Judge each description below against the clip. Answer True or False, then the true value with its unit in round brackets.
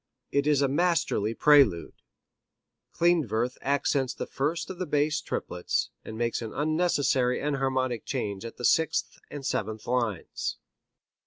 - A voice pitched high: False (135 Hz)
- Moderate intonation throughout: True (4.4 semitones)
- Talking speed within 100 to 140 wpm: True (135 wpm)